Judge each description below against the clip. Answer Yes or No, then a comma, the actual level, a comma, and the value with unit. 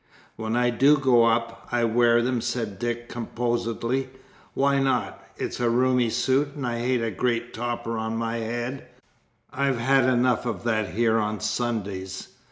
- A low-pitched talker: Yes, low, 120 Hz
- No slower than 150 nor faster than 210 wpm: Yes, average, 165 wpm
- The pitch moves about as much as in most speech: No, narrow, 1.7 semitones